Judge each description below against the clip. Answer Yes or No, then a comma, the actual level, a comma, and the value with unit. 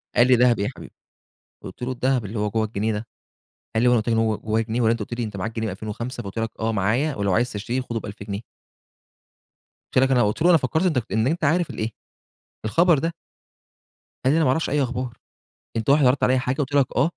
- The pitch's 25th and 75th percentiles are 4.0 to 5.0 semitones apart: No, average, 3.3 semitones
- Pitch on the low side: Yes, low, 120 Hz